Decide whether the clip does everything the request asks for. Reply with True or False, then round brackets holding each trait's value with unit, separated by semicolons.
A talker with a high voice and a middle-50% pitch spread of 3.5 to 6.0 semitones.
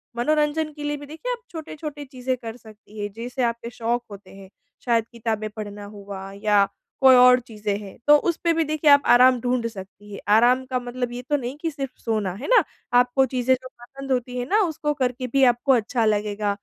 True (245 Hz; 4.1 semitones)